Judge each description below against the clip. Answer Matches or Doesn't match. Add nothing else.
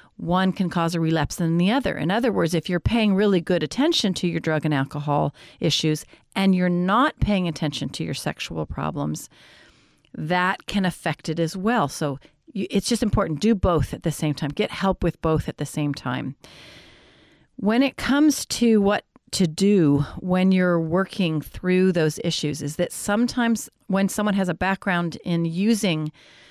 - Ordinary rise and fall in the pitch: Matches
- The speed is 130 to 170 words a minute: Doesn't match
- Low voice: Doesn't match